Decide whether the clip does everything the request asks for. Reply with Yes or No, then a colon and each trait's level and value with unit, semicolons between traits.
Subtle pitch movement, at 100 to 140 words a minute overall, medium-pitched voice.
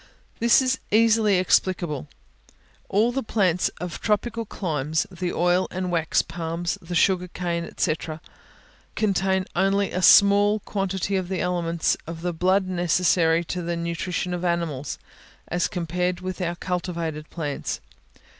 Yes: narrow, 2.3 semitones; slow, 135 wpm; medium, 180 Hz